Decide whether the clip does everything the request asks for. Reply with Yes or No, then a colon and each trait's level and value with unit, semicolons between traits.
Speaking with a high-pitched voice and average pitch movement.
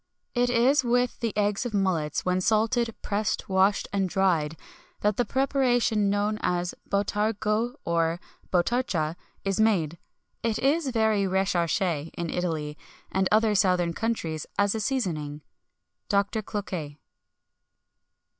Yes: high, 200 Hz; average, 4.2 semitones